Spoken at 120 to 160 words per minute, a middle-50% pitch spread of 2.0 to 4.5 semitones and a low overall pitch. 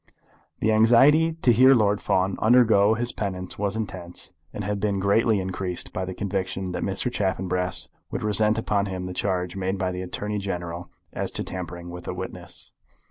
No: average, 180 wpm; average, 2.8 semitones; low, 100 Hz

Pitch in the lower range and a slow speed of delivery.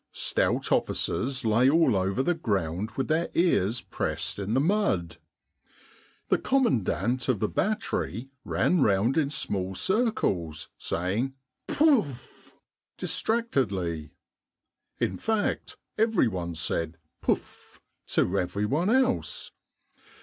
Yes: low, 125 Hz; slow, 115 wpm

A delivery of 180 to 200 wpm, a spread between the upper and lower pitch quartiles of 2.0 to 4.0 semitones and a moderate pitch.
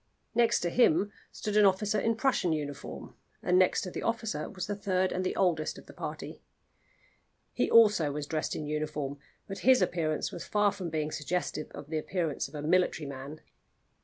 No: average, 190 wpm; average, 5.0 semitones; medium, 175 Hz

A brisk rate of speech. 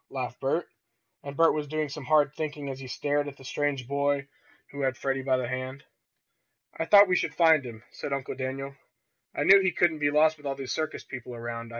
Yes: fast, 220 wpm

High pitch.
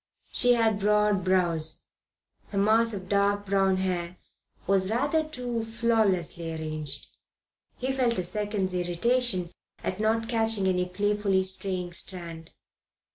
Yes: high, 195 Hz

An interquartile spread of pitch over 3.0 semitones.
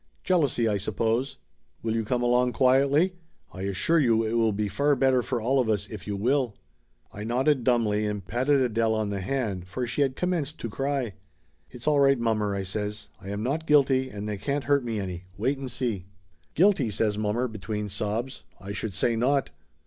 Yes: average, 4.4 semitones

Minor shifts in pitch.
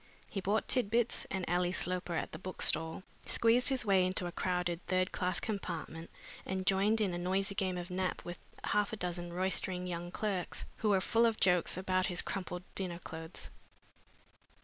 Yes: narrow, 1.9 semitones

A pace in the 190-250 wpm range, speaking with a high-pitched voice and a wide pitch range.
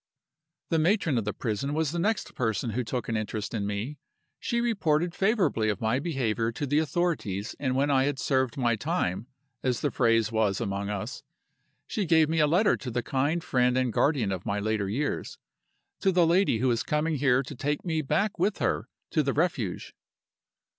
No: average, 195 wpm; low, 135 Hz; wide, 6.1 semitones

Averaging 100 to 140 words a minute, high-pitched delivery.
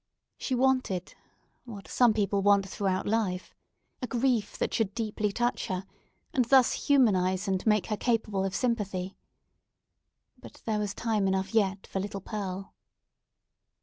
Yes: slow, 135 wpm; high, 205 Hz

